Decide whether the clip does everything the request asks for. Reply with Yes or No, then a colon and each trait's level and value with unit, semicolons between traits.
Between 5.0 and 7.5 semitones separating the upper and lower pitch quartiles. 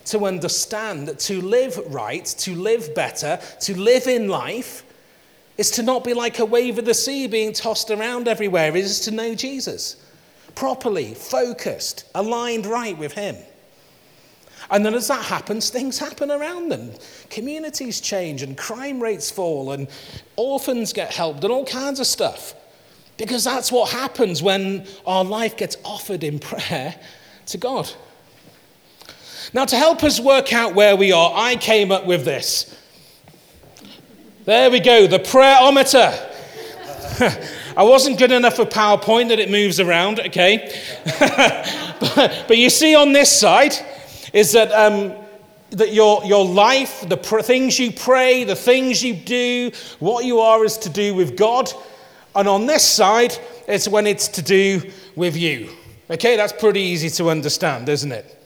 No: average, 4.2 semitones